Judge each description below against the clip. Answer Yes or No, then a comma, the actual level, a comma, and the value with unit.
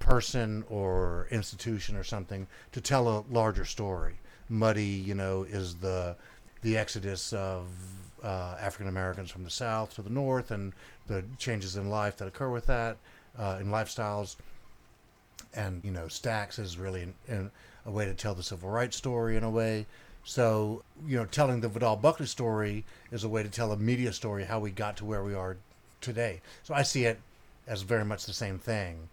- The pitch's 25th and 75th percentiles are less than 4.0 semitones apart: Yes, average, 3.2 semitones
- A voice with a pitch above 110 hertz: No, low, 105 Hz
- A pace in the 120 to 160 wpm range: No, average, 190 wpm